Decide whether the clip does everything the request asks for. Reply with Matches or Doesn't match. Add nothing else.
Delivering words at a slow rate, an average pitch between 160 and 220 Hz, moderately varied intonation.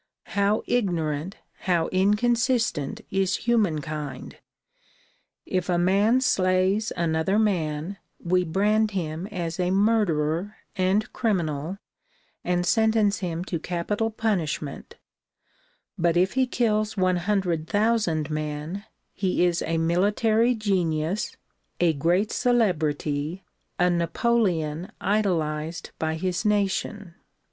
Matches